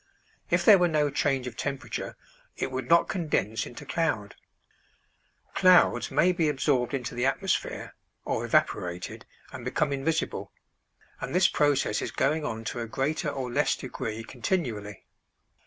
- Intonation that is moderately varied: Yes, average, 5.0 semitones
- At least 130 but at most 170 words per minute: Yes, average, 145 wpm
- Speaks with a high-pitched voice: No, low, 135 Hz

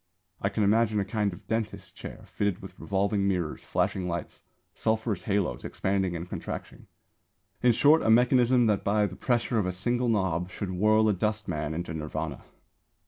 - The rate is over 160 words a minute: Yes, average, 170 wpm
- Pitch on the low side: Yes, low, 100 Hz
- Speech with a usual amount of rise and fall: Yes, average, 3.3 semitones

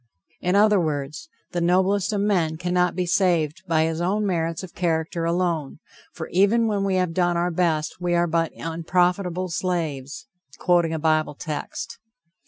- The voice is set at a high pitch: No, medium, 175 Hz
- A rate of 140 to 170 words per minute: Yes, average, 165 wpm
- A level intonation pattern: Yes, narrow, 2.2 semitones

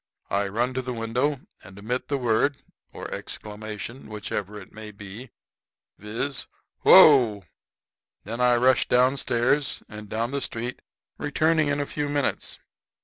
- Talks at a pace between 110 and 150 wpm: Yes, average, 145 wpm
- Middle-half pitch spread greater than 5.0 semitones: No, average, 4.2 semitones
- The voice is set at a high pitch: No, low, 120 Hz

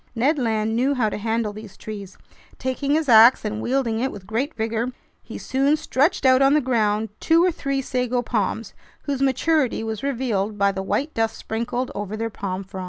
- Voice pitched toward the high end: Yes, high, 235 Hz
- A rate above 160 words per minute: Yes, average, 195 wpm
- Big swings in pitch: No, average, 3.9 semitones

